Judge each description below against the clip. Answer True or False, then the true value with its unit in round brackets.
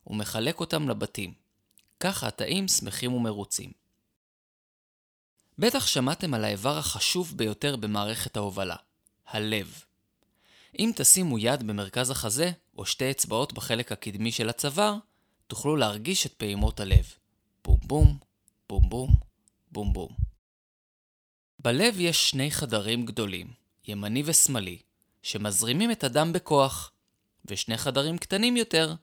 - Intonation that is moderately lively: False (6.1 semitones)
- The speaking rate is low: False (110 wpm)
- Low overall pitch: True (115 Hz)